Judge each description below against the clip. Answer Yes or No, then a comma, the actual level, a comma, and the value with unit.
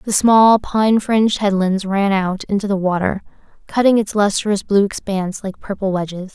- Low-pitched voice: No, high, 200 Hz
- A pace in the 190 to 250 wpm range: No, average, 170 wpm